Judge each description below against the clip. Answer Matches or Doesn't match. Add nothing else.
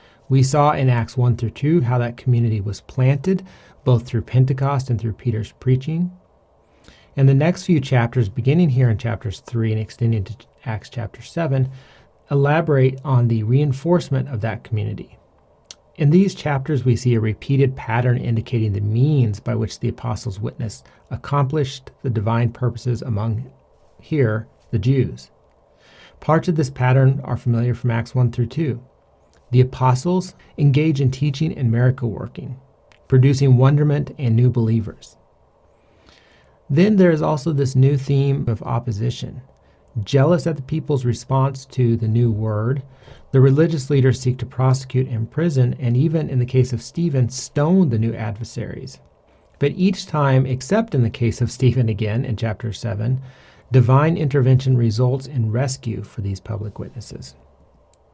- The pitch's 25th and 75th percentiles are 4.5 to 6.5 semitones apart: Doesn't match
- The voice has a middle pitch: Doesn't match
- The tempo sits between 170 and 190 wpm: Doesn't match